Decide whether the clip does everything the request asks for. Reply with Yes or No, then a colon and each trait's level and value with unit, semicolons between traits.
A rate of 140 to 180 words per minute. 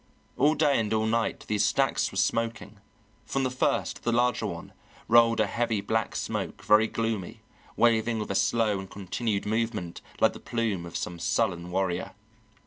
Yes: average, 170 wpm